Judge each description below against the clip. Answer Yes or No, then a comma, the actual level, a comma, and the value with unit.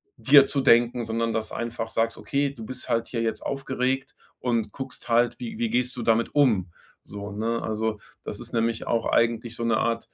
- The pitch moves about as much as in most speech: No, narrow, 2.1 semitones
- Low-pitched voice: Yes, low, 115 Hz